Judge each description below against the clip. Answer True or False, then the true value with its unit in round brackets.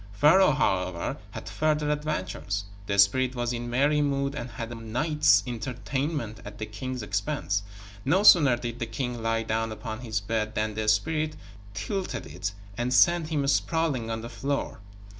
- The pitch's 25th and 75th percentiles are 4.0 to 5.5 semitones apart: True (5.1 semitones)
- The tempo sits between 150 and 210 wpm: True (165 wpm)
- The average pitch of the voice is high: False (120 Hz)